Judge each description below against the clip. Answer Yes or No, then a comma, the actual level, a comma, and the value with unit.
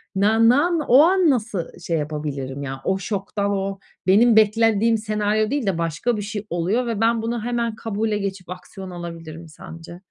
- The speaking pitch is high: Yes, high, 205 Hz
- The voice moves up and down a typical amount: Yes, average, 4.5 semitones